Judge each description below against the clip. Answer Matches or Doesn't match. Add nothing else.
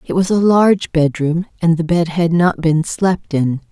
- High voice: Doesn't match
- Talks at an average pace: Doesn't match